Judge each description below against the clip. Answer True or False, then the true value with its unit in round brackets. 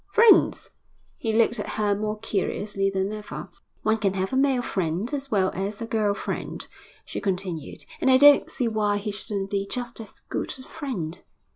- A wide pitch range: False (3.4 semitones)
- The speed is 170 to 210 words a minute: True (185 wpm)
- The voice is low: False (210 Hz)